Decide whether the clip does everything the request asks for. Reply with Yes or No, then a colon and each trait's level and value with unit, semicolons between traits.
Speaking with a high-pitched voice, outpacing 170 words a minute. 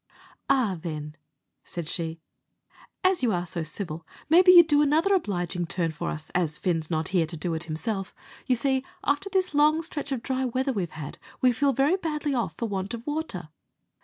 Yes: high, 225 Hz; average, 190 wpm